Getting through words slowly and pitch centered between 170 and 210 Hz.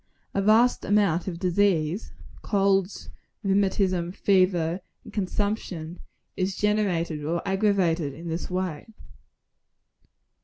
Yes: slow, 100 wpm; medium, 185 Hz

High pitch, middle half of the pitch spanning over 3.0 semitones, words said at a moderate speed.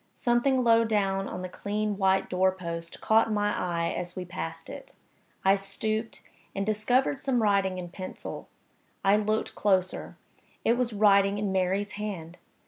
No: high, 200 Hz; average, 2.7 semitones; average, 155 wpm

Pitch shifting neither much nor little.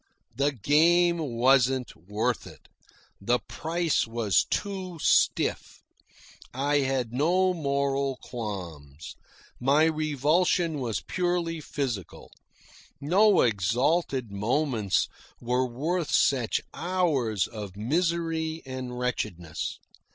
No: wide, 5.9 semitones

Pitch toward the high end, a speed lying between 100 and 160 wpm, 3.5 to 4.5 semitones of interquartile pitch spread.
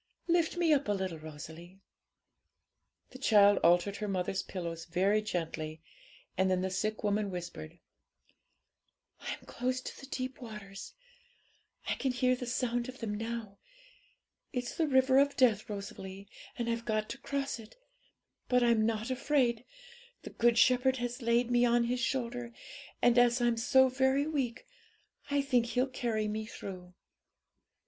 Yes: high, 235 Hz; average, 155 wpm; average, 4.2 semitones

